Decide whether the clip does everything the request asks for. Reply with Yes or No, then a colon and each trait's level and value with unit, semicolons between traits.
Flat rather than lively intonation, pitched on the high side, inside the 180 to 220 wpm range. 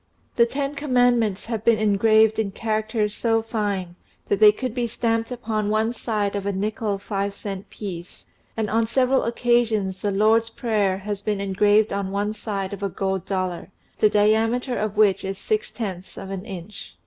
Yes: narrow, 2.3 semitones; high, 215 Hz; average, 185 wpm